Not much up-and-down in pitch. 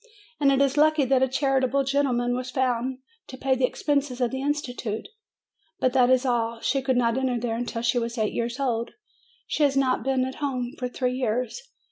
Yes: narrow, 1.9 semitones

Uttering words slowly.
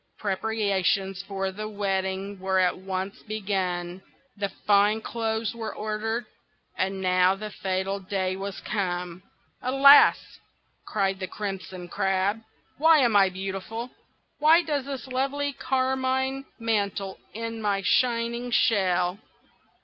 Yes: slow, 120 wpm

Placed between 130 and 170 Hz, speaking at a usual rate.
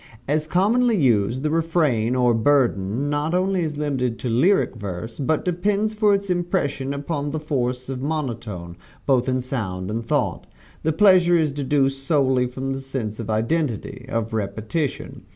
Yes: low, 135 Hz; average, 160 wpm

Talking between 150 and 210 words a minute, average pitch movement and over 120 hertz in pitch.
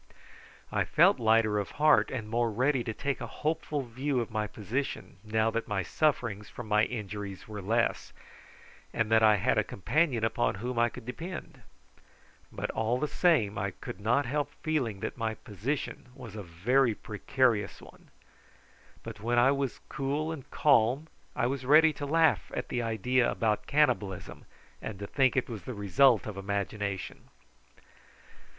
No: average, 165 wpm; average, 4.3 semitones; low, 115 Hz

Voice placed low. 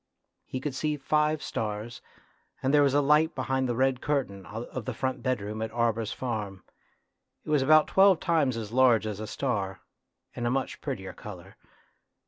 Yes: low, 130 Hz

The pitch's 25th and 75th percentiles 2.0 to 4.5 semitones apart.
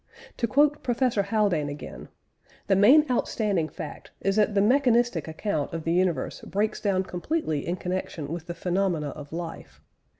No: average, 5.0 semitones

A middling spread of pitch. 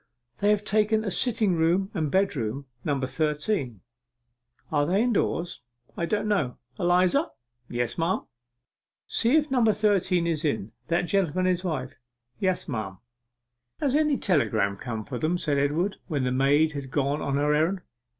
No: wide, 6.0 semitones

